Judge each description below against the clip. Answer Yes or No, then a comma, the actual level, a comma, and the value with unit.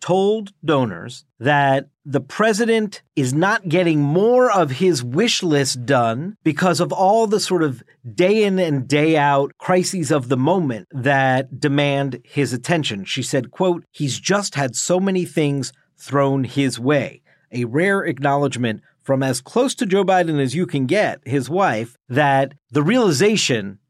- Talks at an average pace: Yes, average, 160 wpm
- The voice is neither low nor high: Yes, medium, 150 Hz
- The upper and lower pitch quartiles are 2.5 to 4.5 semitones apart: No, average, 5.1 semitones